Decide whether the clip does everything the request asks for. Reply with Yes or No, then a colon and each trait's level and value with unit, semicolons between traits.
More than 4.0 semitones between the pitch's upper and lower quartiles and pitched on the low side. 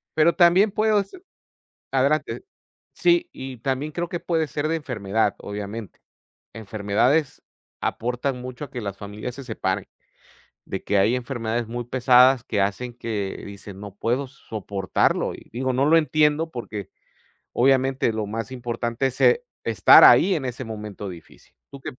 Yes: average, 4.8 semitones; low, 125 Hz